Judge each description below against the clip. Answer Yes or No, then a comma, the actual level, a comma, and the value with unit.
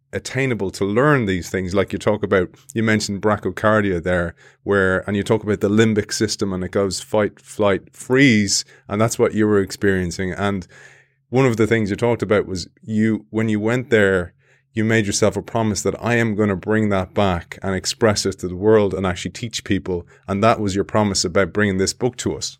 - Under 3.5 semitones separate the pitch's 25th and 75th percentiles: Yes, average, 2.7 semitones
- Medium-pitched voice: No, low, 105 Hz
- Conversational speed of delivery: No, fast, 215 wpm